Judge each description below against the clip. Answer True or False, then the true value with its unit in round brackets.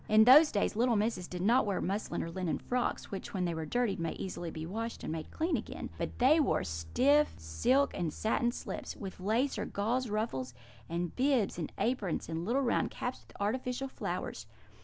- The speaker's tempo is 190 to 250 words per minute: True (200 wpm)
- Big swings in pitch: True (6.2 semitones)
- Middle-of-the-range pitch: False (215 Hz)